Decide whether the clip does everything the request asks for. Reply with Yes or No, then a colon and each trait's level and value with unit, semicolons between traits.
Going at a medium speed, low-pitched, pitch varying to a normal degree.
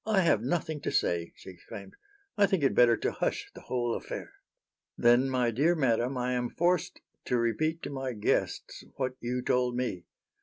Yes: average, 185 wpm; low, 125 Hz; average, 3.9 semitones